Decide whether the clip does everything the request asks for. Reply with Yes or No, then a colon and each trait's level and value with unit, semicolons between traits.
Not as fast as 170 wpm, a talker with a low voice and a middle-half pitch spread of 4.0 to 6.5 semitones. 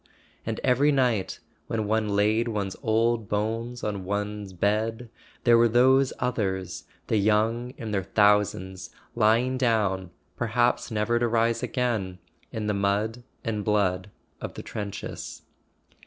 No: average, 140 wpm; low, 110 Hz; narrow, 2.5 semitones